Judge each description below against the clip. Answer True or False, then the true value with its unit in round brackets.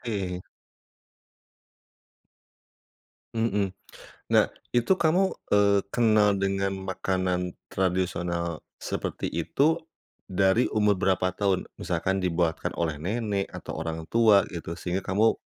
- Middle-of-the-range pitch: False (95 Hz)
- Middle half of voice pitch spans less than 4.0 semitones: True (2.8 semitones)